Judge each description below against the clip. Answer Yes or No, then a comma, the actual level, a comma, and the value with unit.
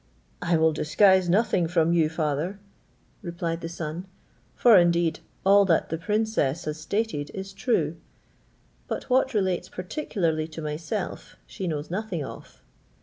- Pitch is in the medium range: Yes, medium, 170 Hz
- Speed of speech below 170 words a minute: Yes, average, 140 wpm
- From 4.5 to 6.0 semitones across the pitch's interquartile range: No, average, 3.6 semitones